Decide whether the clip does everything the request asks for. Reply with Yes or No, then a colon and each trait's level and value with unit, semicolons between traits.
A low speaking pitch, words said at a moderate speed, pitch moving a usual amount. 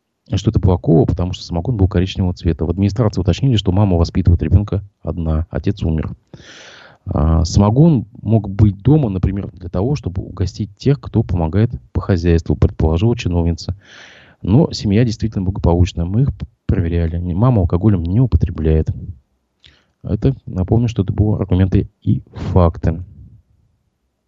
Yes: very low, 95 Hz; average, 135 wpm; average, 4.0 semitones